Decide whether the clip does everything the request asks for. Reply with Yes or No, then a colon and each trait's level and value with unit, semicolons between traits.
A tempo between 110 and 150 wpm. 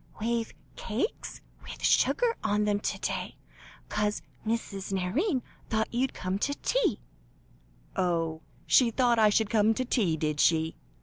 Yes: average, 140 wpm